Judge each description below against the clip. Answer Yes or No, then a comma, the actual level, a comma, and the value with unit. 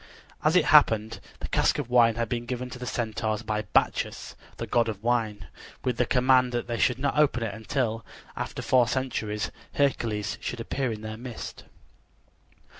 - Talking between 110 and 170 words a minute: No, average, 180 wpm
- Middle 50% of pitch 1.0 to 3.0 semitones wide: Yes, narrow, 2.4 semitones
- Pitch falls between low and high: No, low, 120 Hz